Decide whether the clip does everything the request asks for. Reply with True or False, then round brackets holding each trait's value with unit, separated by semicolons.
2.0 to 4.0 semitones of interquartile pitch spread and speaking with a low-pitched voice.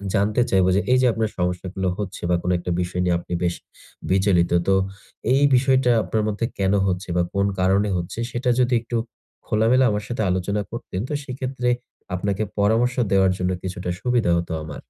False (4.6 semitones; 100 Hz)